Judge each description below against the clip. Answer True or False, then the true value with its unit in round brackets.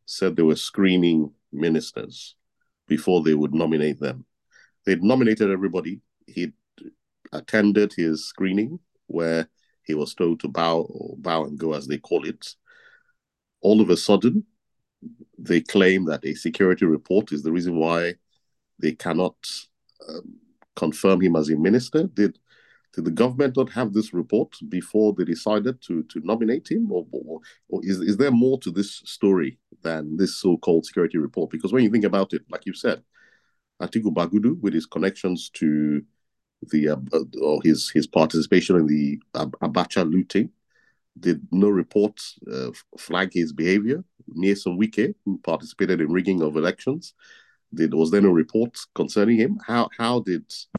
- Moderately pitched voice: False (95 Hz)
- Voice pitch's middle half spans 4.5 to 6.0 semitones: True (5.0 semitones)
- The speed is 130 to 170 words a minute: True (160 wpm)